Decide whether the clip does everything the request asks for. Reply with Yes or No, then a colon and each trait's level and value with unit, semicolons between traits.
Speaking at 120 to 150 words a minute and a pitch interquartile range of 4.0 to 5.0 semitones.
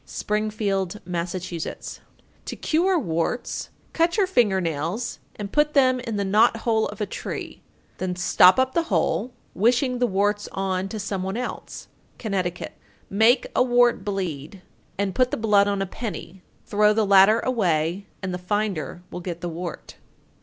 No: average, 165 wpm; average, 4.4 semitones